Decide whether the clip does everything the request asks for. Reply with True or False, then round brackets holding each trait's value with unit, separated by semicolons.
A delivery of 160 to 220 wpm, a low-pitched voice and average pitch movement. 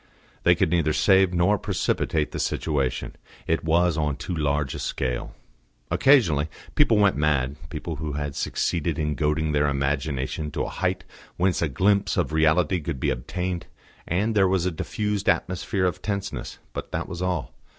True (170 wpm; 80 Hz; 4.0 semitones)